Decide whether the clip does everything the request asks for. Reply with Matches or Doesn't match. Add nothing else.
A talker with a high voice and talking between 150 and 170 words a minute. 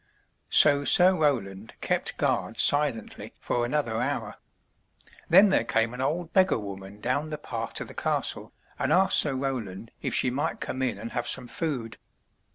Doesn't match